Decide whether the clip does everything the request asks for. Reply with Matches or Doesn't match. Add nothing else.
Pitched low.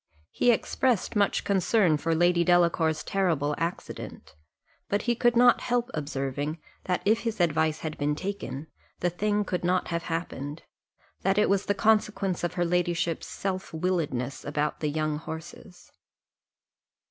Doesn't match